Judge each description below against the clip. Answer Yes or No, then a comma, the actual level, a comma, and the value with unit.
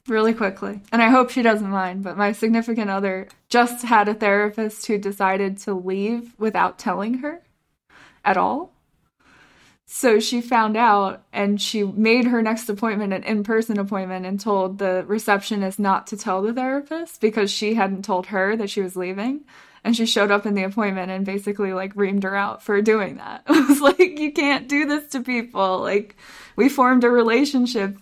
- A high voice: Yes, high, 215 Hz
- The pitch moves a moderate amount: Yes, average, 3.1 semitones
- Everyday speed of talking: Yes, average, 185 wpm